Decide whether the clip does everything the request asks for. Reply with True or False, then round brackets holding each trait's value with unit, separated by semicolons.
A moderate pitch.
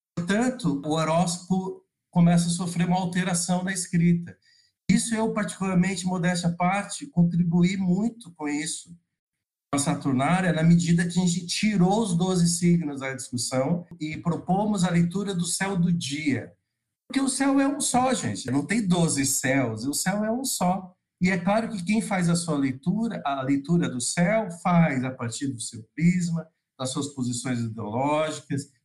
True (175 Hz)